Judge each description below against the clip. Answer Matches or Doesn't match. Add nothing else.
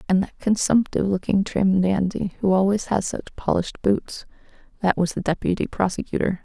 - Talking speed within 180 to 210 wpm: Doesn't match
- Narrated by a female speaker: Matches